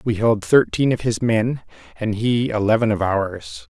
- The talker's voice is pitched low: Yes, low, 110 Hz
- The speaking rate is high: No, average, 175 wpm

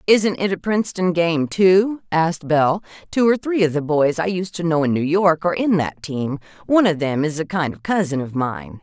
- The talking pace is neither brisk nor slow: No, fast, 240 wpm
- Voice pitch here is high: No, medium, 170 Hz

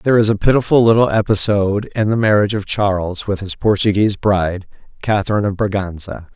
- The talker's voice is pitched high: No, low, 100 Hz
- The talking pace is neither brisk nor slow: Yes, average, 170 wpm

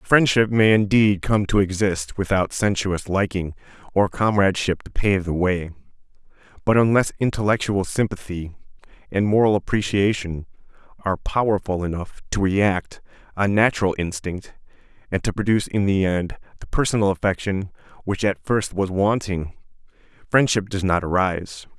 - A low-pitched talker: Yes, low, 100 Hz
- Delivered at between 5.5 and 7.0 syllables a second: No, 5.0 syllables/s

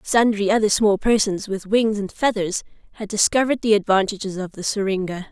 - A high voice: Yes, high, 205 Hz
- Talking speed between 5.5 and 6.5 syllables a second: Yes, 5.6 syllables/s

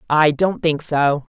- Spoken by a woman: Yes, female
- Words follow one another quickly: No, average, 180 wpm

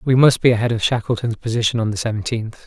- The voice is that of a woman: No, male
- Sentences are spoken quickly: Yes, fast, 225 wpm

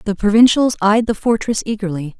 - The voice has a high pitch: Yes, high, 210 Hz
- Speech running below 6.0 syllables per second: Yes, 5.6 syllables/s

